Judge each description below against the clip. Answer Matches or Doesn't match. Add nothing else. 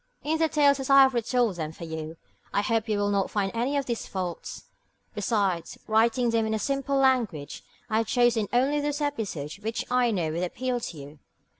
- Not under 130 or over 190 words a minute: Doesn't match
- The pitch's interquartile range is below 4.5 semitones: Doesn't match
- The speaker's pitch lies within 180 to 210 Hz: Doesn't match